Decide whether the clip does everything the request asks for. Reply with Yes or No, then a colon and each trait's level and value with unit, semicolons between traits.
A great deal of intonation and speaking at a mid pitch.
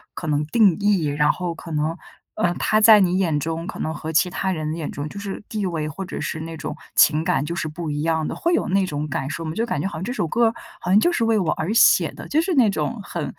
No: average, 4.6 semitones; medium, 170 Hz